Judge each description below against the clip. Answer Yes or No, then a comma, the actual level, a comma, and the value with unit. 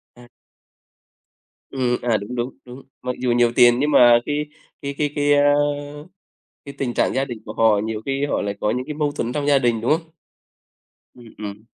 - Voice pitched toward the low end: Yes, low, 125 Hz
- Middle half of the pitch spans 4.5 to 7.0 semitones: No, average, 3.4 semitones